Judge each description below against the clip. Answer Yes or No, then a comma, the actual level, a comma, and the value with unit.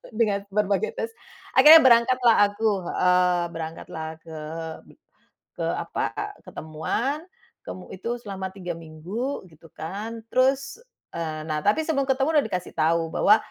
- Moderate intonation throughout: No, wide, 6.5 semitones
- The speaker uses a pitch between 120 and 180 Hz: No, high, 200 Hz